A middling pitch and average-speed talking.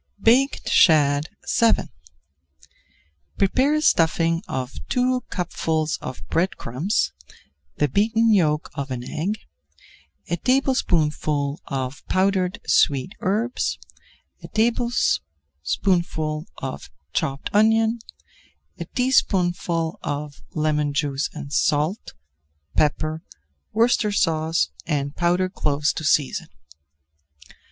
No: medium, 165 Hz; slow, 95 wpm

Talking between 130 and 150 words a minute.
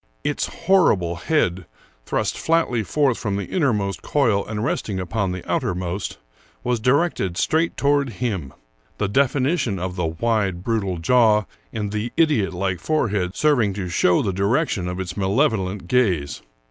Yes: average, 145 wpm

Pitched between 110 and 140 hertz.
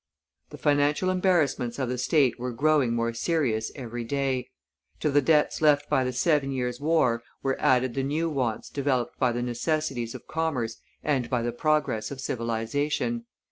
Yes: low, 135 Hz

